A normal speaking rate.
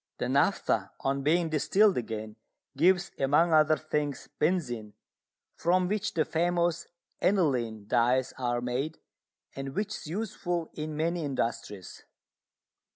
No: slow, 120 wpm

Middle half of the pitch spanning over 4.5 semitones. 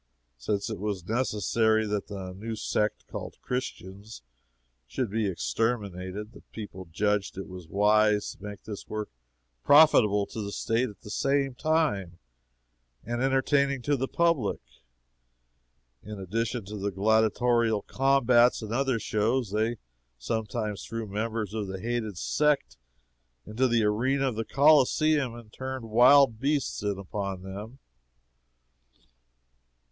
No: average, 3.6 semitones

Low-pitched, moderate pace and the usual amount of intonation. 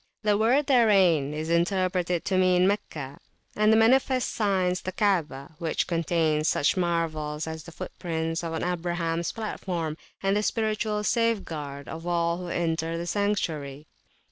No: medium, 175 Hz; average, 145 wpm; average, 4.0 semitones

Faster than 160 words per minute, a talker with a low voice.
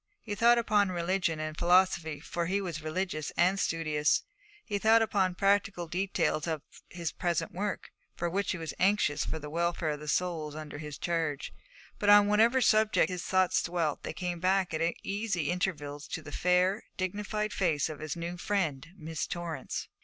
No: average, 175 wpm; medium, 175 Hz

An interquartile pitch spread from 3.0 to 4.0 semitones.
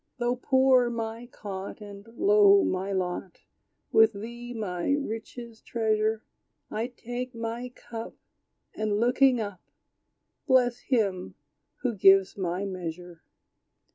Yes: average, 3.7 semitones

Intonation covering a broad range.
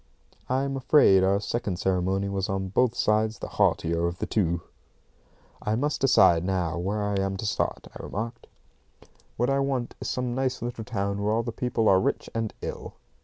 No: average, 4.1 semitones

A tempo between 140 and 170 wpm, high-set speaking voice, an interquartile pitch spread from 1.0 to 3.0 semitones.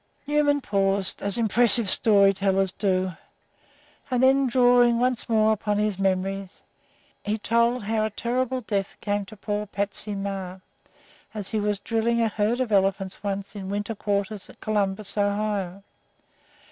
Yes: average, 145 wpm; high, 205 Hz; average, 2.7 semitones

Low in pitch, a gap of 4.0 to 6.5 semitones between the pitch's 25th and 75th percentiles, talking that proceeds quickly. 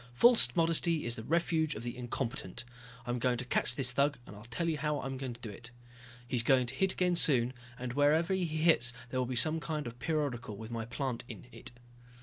Yes: low, 130 Hz; average, 4.7 semitones; fast, 220 wpm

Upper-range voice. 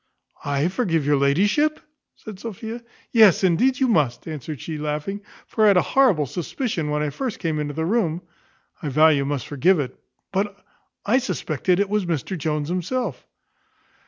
No: medium, 175 Hz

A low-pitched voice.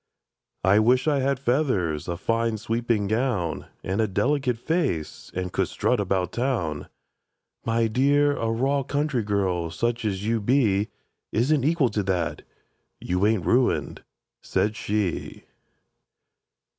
Yes: low, 115 Hz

